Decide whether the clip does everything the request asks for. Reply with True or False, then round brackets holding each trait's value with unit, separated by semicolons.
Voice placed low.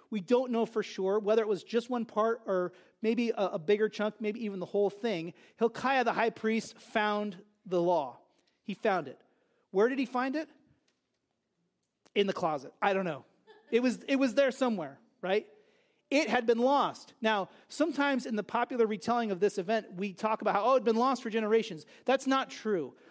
False (225 Hz)